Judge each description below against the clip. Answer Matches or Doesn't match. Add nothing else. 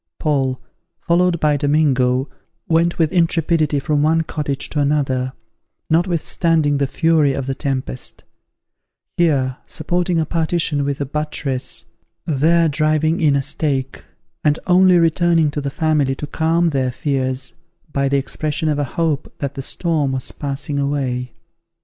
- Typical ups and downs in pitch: Matches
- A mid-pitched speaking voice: Matches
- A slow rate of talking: Doesn't match